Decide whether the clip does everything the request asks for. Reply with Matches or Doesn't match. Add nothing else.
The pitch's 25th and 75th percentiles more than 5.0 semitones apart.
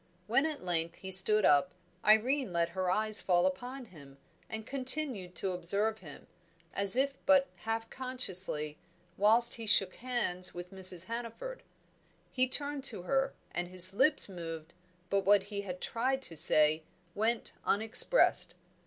Matches